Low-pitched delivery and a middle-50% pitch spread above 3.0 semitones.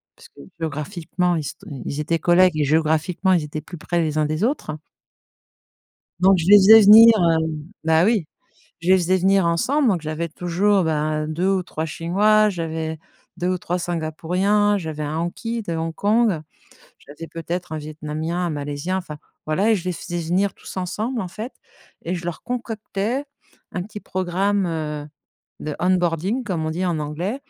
No: medium, 175 Hz; average, 3.6 semitones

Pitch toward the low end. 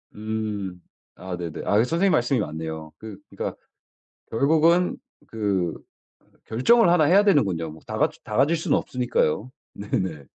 Yes: low, 110 Hz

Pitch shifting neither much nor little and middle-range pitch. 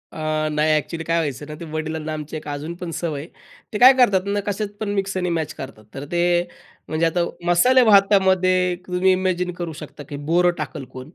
Yes: average, 3.4 semitones; medium, 170 Hz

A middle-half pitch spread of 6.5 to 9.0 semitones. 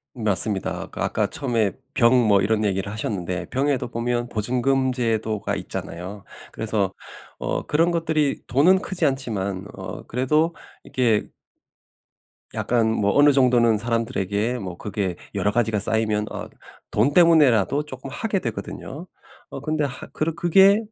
No: average, 5.2 semitones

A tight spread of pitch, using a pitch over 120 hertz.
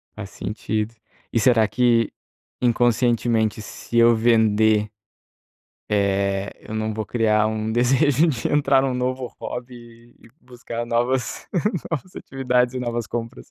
No: narrow, 2.3 semitones; low, 115 Hz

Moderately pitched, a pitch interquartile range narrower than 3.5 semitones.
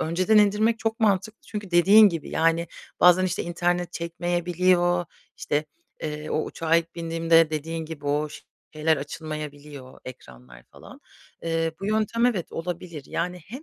Yes: medium, 170 Hz; average, 2.8 semitones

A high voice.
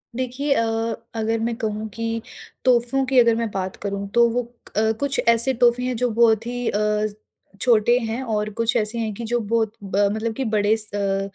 Yes: high, 230 Hz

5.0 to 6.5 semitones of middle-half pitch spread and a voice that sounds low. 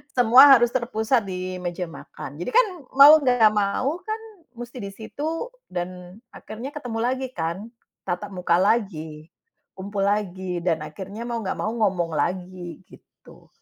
No: wide, 5.5 semitones; high, 200 Hz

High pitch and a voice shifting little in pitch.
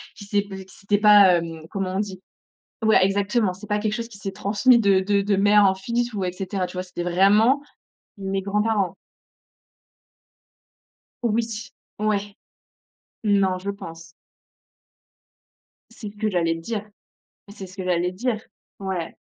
Yes: high, 200 Hz; narrow, 2.0 semitones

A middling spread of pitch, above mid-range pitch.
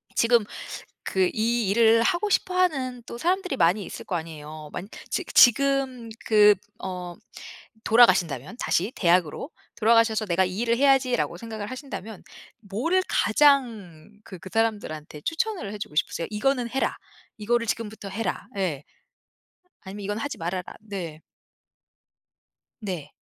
Yes: average, 5.0 semitones; high, 215 Hz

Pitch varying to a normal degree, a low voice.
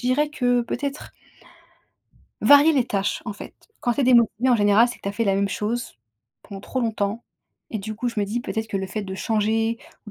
No: average, 3.1 semitones; high, 225 Hz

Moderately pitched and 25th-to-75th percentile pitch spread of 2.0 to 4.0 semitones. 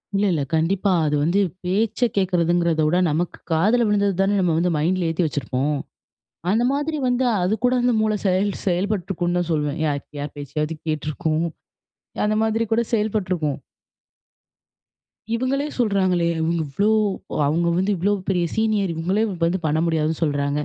No: medium, 180 Hz; average, 4.5 semitones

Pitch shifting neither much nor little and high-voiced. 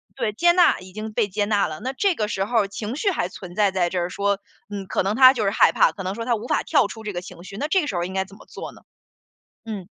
Yes: average, 3.5 semitones; high, 205 Hz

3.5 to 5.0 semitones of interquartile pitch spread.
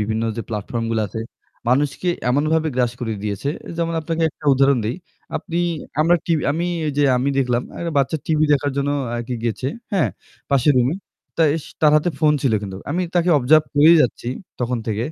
Yes: average, 4.7 semitones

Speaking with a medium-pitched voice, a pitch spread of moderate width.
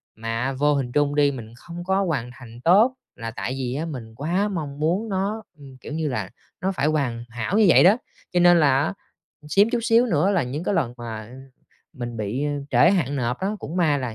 No: medium, 145 Hz; wide, 6.3 semitones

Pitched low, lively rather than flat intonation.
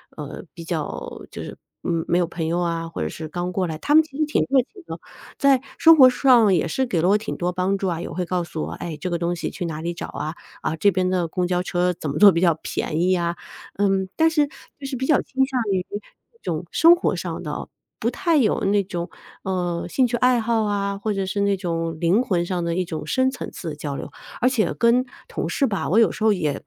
No: medium, 185 Hz; wide, 5.7 semitones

